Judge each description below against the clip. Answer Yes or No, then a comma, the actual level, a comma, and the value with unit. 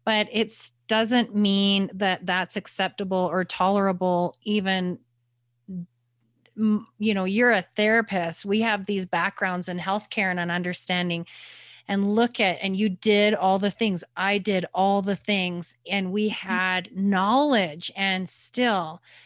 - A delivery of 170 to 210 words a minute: No, slow, 135 wpm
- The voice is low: No, high, 195 Hz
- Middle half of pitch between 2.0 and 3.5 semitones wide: Yes, average, 2.7 semitones